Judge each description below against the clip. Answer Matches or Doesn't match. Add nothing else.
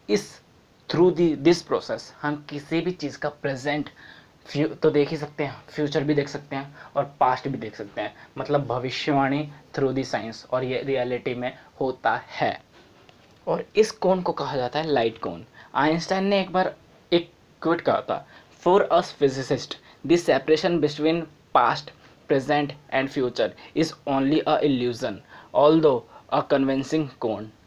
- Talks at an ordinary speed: Matches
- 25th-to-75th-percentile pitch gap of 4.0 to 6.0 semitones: Doesn't match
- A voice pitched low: Doesn't match